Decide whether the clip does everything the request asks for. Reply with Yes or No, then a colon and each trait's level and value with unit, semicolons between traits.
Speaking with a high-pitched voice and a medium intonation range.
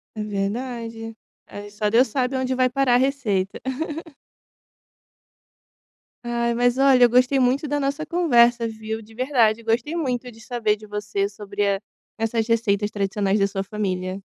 Yes: high, 230 Hz; average, 3.4 semitones